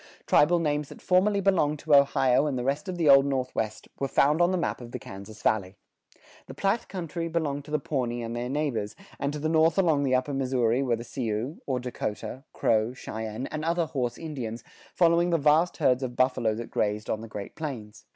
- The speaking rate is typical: No, fast, 210 wpm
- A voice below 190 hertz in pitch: Yes, low, 135 Hz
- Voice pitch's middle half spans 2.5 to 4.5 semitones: No, average, 4.9 semitones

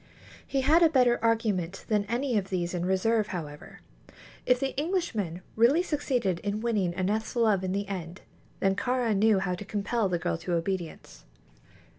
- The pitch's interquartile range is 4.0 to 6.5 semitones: Yes, average, 4.5 semitones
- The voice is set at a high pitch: Yes, high, 205 Hz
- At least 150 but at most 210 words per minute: Yes, average, 170 wpm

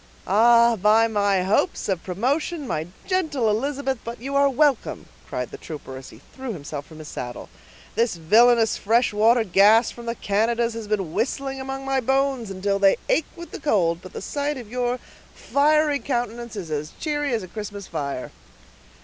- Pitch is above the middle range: Yes, high, 230 Hz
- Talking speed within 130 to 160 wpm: No, average, 180 wpm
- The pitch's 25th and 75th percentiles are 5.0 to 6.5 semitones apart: Yes, average, 5.3 semitones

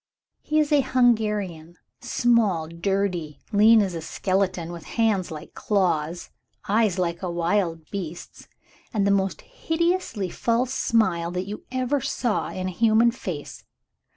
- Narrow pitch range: No, average, 5.0 semitones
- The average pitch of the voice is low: No, high, 200 Hz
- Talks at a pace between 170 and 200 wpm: No, slow, 135 wpm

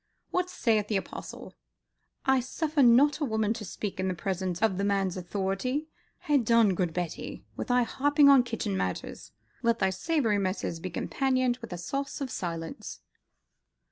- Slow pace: No, average, 165 wpm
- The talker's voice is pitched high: Yes, high, 220 Hz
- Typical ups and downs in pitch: No, wide, 6.0 semitones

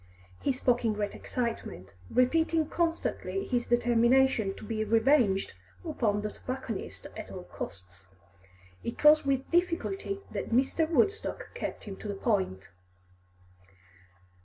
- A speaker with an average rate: No, slow, 125 wpm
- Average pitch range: No, wide, 6.3 semitones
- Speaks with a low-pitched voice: No, high, 240 Hz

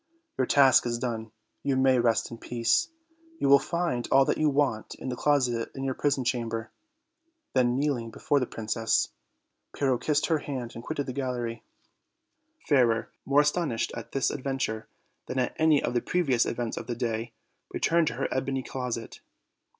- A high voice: No, low, 130 Hz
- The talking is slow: No, average, 170 wpm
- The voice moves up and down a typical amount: Yes, average, 3.1 semitones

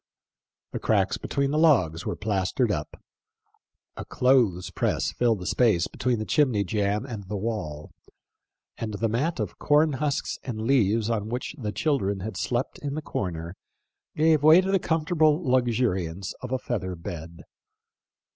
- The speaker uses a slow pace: No, average, 155 wpm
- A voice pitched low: Yes, low, 115 Hz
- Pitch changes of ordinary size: No, wide, 6.2 semitones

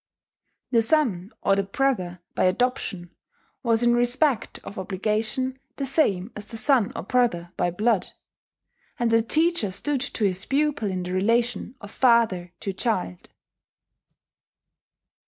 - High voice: Yes, high, 225 Hz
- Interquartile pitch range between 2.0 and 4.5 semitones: No, average, 5.1 semitones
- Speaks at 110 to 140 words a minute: Yes, slow, 135 wpm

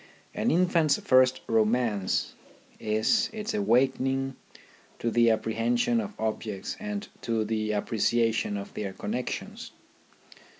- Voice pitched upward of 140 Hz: No, low, 115 Hz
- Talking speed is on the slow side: Yes, slow, 110 wpm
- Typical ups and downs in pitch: Yes, average, 3.6 semitones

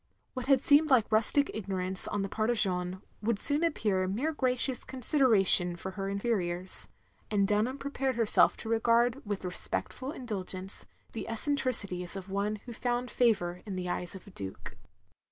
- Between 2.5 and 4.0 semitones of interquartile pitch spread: No, average, 5.0 semitones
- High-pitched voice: Yes, high, 215 Hz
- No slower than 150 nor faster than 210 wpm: Yes, average, 170 wpm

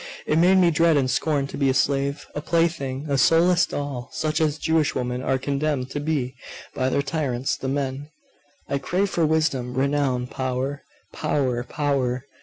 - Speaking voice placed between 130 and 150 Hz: Yes, medium, 140 Hz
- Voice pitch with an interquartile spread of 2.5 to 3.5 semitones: Yes, average, 3.1 semitones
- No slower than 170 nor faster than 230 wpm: Yes, average, 180 wpm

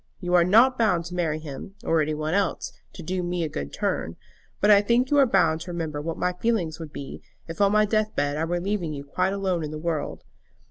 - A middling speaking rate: No, fast, 245 wpm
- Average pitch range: Yes, average, 4.2 semitones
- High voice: No, medium, 175 Hz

